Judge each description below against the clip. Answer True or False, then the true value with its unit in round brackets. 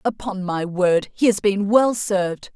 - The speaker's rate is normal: True (190 wpm)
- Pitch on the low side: False (200 Hz)